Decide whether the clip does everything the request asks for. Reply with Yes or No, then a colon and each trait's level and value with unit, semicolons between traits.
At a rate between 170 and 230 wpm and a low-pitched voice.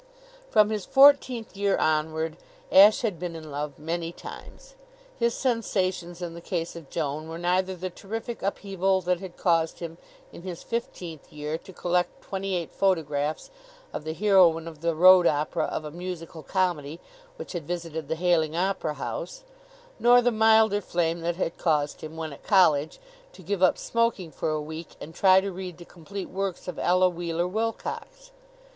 No: average, 175 wpm; medium, 175 Hz